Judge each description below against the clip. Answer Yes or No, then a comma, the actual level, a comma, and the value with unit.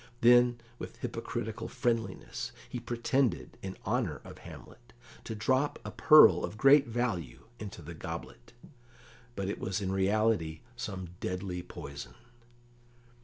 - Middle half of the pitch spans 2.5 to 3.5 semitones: No, average, 4.6 semitones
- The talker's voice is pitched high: No, low, 110 Hz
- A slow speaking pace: Yes, slow, 125 wpm